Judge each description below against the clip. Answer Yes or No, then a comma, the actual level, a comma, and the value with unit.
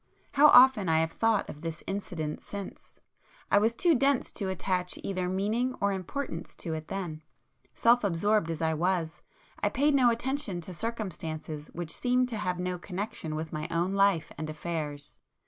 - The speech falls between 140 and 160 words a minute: No, average, 170 wpm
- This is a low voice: No, medium, 185 Hz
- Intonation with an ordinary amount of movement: No, wide, 5.7 semitones